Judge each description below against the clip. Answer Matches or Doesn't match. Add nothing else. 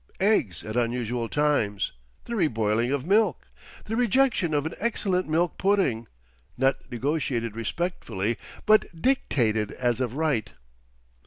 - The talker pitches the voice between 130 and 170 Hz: Matches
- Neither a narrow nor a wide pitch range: Doesn't match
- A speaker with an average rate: Doesn't match